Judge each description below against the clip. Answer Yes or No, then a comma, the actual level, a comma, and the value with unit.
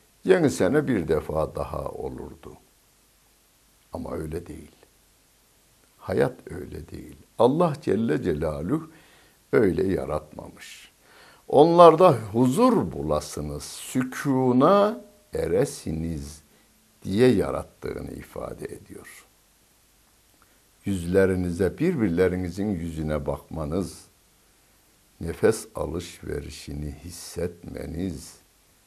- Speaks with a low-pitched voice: Yes, very low, 95 Hz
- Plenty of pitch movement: Yes, wide, 8.4 semitones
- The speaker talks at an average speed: No, slow, 70 wpm